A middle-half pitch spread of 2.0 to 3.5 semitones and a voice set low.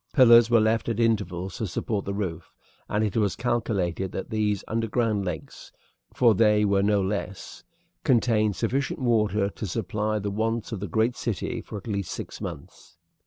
Yes: narrow, 2.5 semitones; low, 105 Hz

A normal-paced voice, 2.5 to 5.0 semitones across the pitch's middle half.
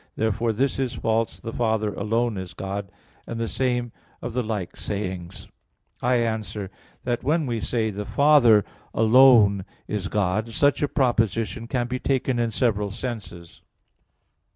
Yes: average, 150 wpm; average, 2.9 semitones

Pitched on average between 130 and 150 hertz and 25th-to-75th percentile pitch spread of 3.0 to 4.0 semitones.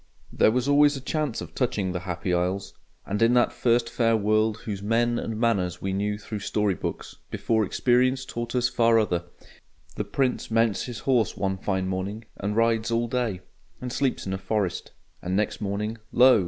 No: low, 110 Hz; average, 3.5 semitones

